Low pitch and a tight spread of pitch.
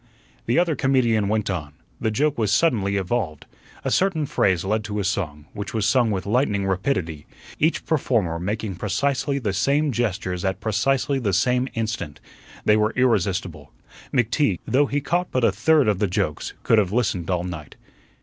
No: low, 110 Hz; average, 5.3 semitones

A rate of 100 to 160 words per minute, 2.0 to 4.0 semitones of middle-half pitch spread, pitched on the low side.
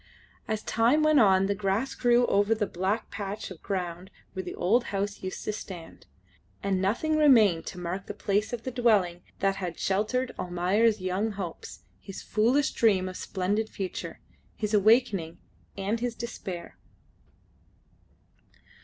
No: average, 150 wpm; average, 3.3 semitones; high, 200 Hz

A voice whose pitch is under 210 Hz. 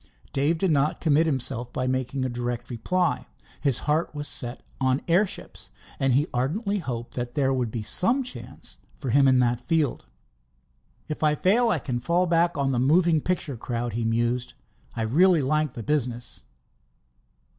Yes: low, 135 Hz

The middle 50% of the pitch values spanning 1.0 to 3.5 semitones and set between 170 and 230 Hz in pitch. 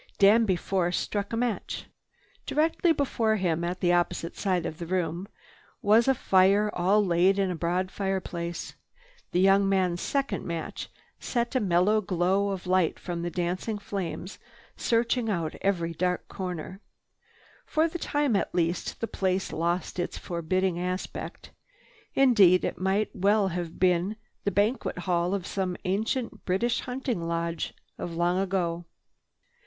Yes: average, 2.9 semitones; medium, 185 Hz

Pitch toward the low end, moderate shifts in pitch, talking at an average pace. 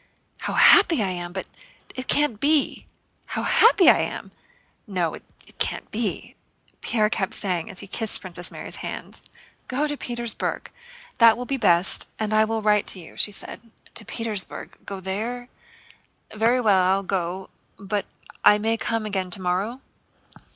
No: high, 210 Hz; average, 3.8 semitones; average, 160 wpm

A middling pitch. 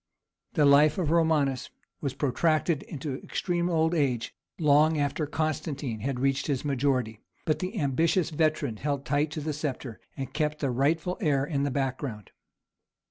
Yes: medium, 145 Hz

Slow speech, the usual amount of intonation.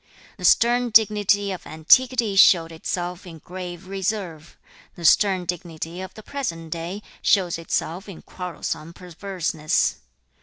Yes: slow, 125 wpm; average, 3.3 semitones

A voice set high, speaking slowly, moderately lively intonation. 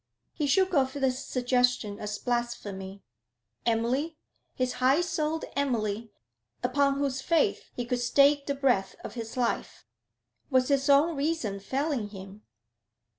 Yes: very high, 255 Hz; slow, 130 wpm; average, 3.6 semitones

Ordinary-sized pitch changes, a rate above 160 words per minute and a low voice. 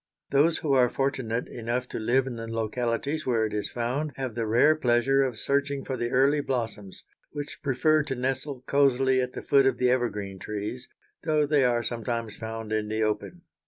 Yes: average, 3.3 semitones; average, 195 wpm; low, 125 Hz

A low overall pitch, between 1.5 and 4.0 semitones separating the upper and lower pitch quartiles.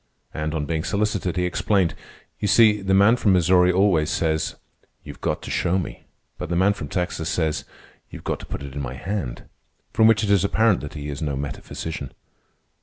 No: very low, 90 Hz; average, 4.5 semitones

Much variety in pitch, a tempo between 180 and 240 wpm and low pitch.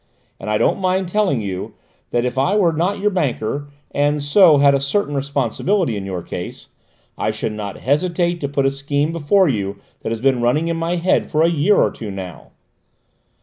No: wide, 6.2 semitones; average, 200 wpm; medium, 145 Hz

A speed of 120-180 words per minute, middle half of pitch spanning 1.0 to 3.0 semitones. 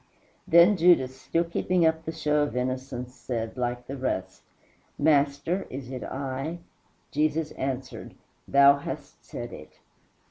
No: slow, 135 wpm; average, 3.8 semitones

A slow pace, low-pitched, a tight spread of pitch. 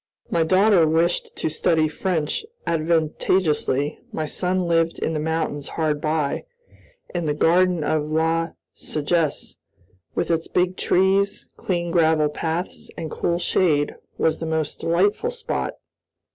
No: slow, 130 wpm; medium, 165 Hz; narrow, 2.2 semitones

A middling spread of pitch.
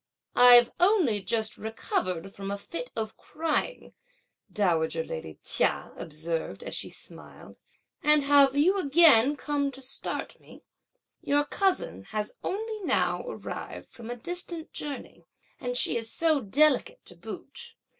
No: wide, 7.2 semitones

